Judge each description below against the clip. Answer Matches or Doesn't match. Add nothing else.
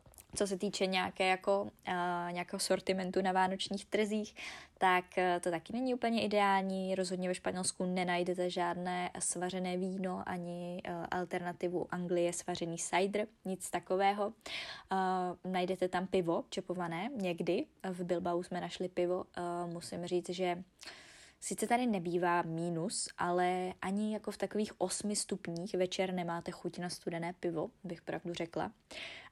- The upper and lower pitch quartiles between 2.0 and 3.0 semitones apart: Doesn't match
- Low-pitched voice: Doesn't match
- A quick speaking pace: Doesn't match